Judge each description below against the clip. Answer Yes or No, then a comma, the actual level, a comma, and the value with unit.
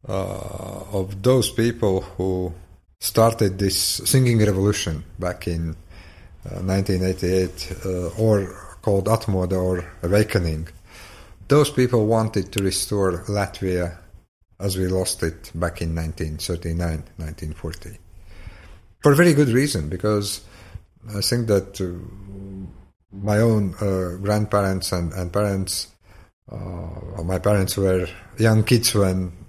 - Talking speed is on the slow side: Yes, slow, 115 wpm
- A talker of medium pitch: No, very low, 95 Hz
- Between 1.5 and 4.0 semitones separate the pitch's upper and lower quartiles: Yes, narrow, 2.6 semitones